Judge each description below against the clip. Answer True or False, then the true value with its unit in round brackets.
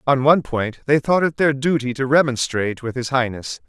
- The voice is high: False (135 Hz)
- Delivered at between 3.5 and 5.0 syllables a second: False (5.5 syllables/s)